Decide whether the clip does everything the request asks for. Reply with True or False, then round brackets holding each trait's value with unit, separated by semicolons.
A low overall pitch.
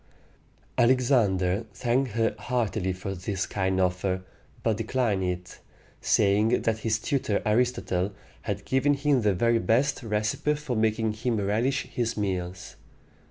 True (110 Hz)